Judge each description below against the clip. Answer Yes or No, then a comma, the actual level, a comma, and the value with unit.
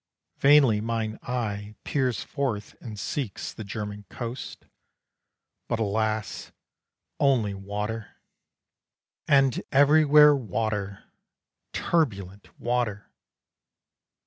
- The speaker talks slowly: Yes, slow, 80 wpm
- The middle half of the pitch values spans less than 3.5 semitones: No, average, 4.3 semitones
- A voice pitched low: Yes, low, 110 Hz